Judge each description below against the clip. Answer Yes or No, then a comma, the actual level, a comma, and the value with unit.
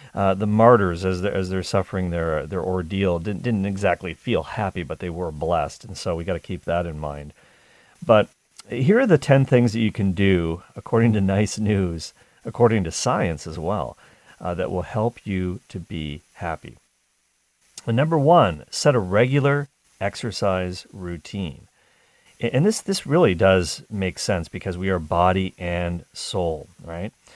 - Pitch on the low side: Yes, very low, 95 Hz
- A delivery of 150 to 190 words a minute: Yes, average, 170 wpm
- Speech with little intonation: No, average, 4.5 semitones